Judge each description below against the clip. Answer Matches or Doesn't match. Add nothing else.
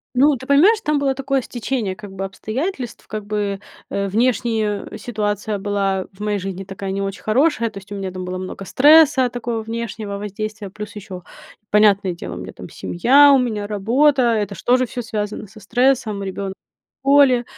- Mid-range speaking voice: Doesn't match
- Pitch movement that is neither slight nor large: Matches